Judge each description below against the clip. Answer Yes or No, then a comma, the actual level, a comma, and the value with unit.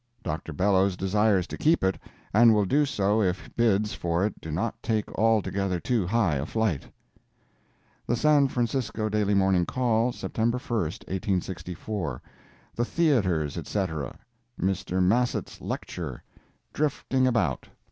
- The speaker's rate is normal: No, slow, 125 wpm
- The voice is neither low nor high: No, low, 105 Hz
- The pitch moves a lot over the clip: No, average, 4.3 semitones